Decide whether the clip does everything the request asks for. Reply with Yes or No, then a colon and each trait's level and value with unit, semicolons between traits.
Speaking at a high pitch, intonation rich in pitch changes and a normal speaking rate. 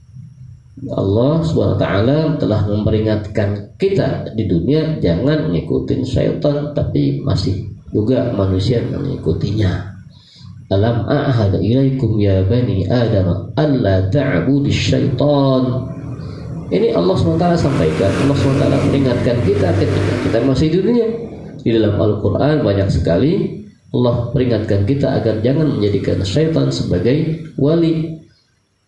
No: low, 125 Hz; wide, 5.7 semitones; average, 95 wpm